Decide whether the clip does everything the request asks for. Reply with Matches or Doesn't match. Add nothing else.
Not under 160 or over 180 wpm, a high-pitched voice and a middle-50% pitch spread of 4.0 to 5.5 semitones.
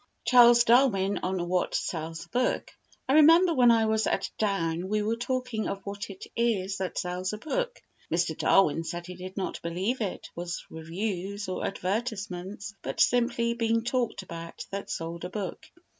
Matches